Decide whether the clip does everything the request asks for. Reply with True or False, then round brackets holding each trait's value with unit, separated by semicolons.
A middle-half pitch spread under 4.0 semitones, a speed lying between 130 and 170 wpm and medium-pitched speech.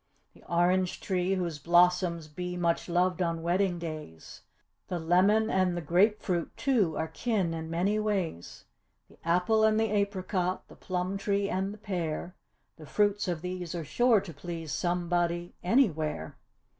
True (2.7 semitones; 155 wpm; 180 Hz)